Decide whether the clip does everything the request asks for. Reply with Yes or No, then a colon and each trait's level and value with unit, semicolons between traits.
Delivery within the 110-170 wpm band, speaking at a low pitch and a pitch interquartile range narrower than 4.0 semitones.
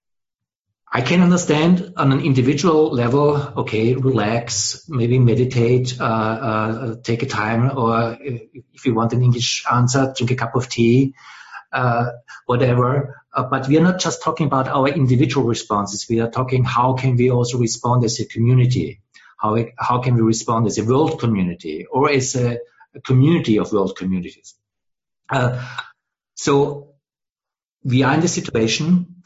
Yes: average, 155 wpm; low, 125 Hz; average, 3.3 semitones